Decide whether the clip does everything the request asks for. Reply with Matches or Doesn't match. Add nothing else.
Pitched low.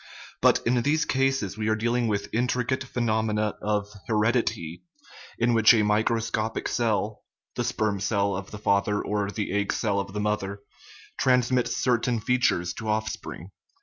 Matches